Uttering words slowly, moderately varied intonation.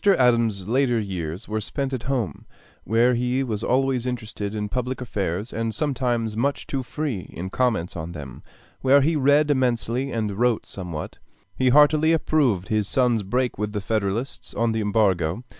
No: average, 165 wpm; average, 4.1 semitones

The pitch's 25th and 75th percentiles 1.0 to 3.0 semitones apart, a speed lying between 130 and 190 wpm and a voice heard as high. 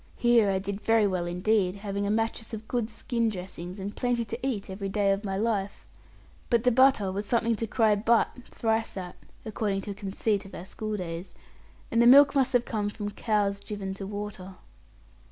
No: average, 2.7 semitones; average, 200 wpm; high, 210 Hz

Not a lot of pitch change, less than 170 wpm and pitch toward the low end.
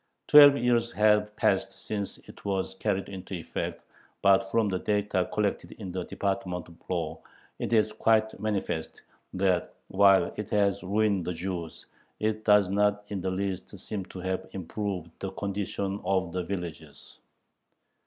Yes: narrow, 2.2 semitones; average, 155 wpm; low, 100 Hz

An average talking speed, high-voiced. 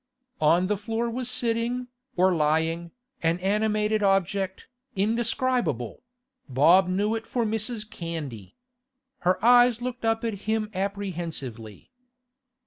No: slow, 115 wpm; high, 200 Hz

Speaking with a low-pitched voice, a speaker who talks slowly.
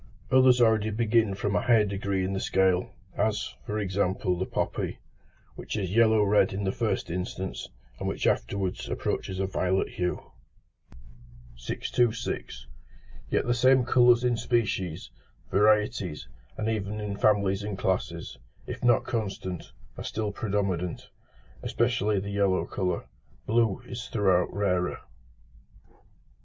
Yes: low, 100 Hz; slow, 130 wpm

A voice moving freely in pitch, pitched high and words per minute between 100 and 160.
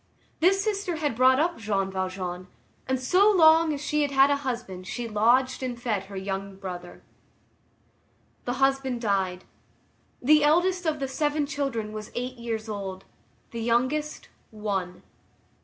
Yes: wide, 6.7 semitones; high, 245 Hz; average, 145 wpm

